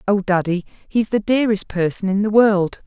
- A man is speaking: No, female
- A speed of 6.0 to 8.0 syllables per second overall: No, 5.1 syllables/s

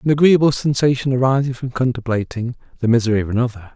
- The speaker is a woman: No, male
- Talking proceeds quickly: No, average, 160 wpm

